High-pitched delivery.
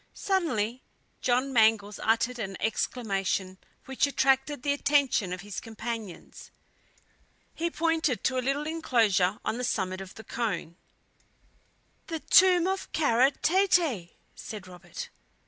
Yes: high, 240 Hz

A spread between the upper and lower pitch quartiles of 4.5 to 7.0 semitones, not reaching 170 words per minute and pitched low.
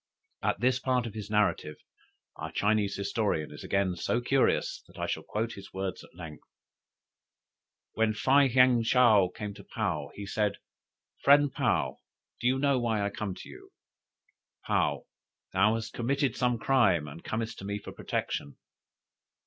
No: average, 4.1 semitones; average, 160 wpm; low, 110 Hz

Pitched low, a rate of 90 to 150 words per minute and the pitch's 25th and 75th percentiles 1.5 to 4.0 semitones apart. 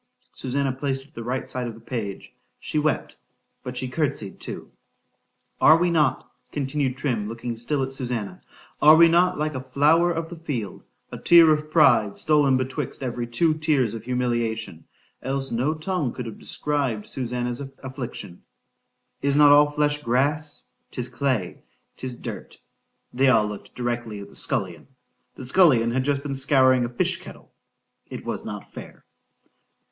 Yes: low, 130 Hz; average, 140 wpm; average, 3.7 semitones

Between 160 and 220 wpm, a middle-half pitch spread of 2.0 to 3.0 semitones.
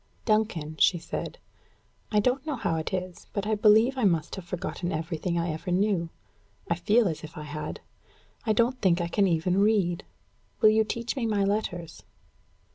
No: average, 185 wpm; average, 4.2 semitones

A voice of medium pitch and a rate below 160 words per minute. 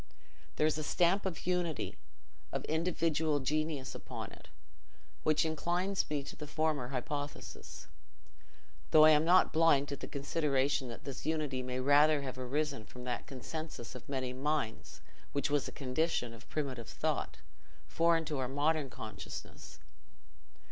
Yes: medium, 145 Hz; average, 150 wpm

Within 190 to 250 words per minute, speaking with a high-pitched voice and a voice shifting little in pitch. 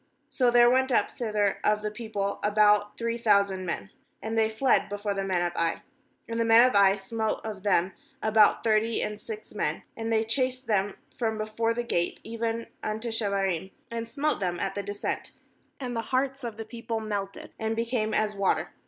Yes: average, 195 wpm; high, 220 Hz; narrow, 2.3 semitones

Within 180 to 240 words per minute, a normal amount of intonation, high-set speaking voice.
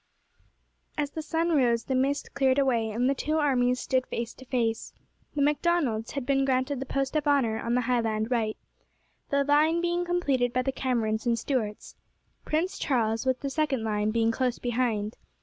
Yes: average, 185 wpm; average, 3.5 semitones; very high, 255 Hz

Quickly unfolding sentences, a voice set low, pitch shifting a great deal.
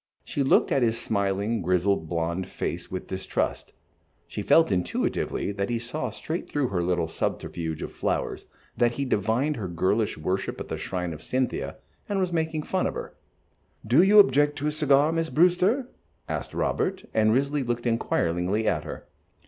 No: average, 175 wpm; low, 115 Hz; wide, 8.1 semitones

